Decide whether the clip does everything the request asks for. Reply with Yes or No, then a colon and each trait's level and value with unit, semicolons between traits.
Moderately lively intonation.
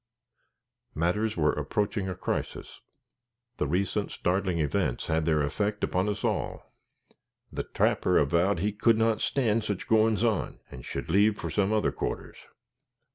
Yes: average, 4.3 semitones